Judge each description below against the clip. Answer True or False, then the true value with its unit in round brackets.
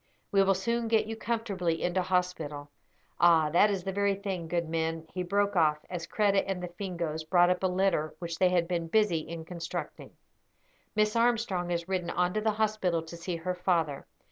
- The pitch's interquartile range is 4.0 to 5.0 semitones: False (3.0 semitones)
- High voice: False (180 Hz)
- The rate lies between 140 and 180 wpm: False (195 wpm)